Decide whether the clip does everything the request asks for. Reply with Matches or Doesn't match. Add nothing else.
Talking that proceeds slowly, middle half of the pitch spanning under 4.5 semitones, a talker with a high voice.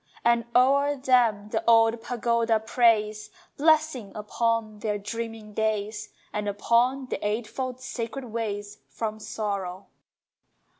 Matches